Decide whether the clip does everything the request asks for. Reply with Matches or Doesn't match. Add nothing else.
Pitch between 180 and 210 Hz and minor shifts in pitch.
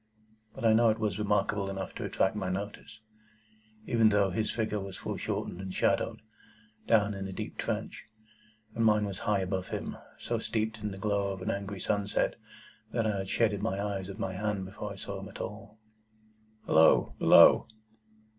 Doesn't match